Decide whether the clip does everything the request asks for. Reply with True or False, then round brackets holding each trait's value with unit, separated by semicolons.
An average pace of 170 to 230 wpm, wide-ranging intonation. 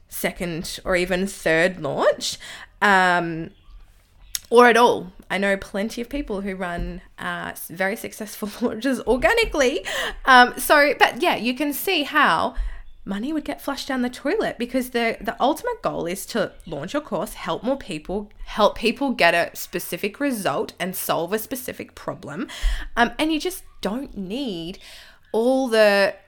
False (155 wpm; 6.4 semitones)